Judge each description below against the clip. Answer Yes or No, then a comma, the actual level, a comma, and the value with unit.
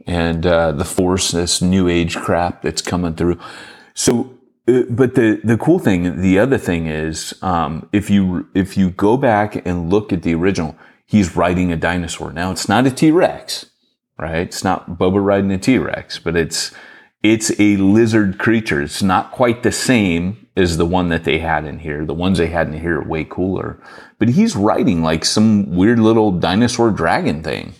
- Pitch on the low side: Yes, very low, 90 Hz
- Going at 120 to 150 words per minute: No, average, 190 wpm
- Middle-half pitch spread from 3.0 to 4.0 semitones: Yes, average, 3.4 semitones